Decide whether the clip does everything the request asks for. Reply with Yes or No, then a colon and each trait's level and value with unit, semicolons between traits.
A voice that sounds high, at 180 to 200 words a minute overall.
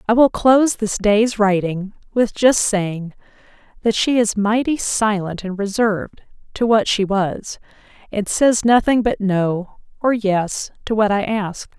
No: high, 210 Hz; average, 160 wpm